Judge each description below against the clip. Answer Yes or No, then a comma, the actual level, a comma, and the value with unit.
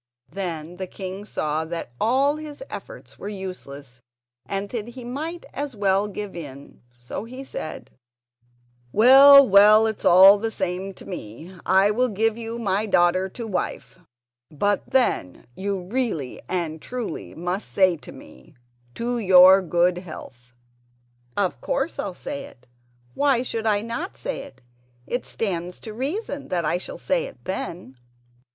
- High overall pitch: Yes, high, 200 Hz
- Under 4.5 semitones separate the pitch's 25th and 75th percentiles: No, average, 5.2 semitones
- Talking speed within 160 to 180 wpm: No, average, 150 wpm